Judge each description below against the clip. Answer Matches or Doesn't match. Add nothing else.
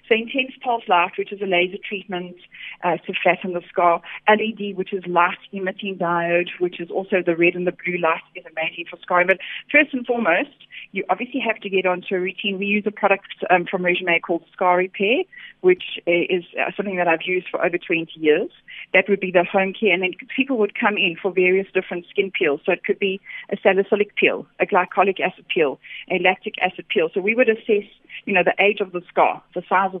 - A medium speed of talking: Doesn't match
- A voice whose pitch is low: Doesn't match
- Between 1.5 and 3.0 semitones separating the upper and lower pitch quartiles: Matches